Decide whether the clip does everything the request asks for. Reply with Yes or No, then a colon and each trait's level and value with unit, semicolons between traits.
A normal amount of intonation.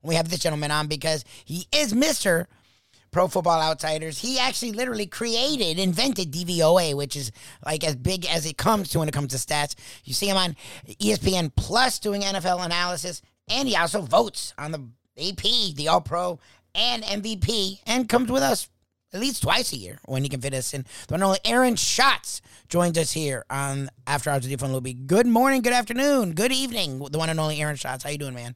No: wide, 6.7 semitones